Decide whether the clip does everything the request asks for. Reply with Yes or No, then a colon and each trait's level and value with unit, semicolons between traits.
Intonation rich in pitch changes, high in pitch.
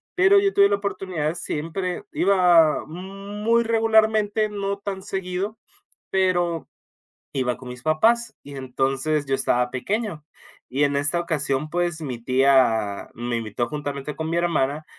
No: wide, 6.6 semitones; medium, 165 Hz